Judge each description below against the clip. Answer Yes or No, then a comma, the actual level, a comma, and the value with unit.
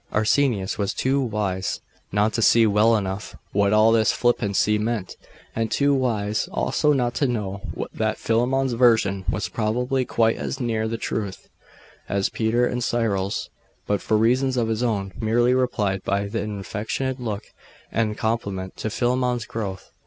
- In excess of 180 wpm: No, average, 160 wpm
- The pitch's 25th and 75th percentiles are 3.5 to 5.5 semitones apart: No, average, 3.0 semitones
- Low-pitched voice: Yes, low, 110 Hz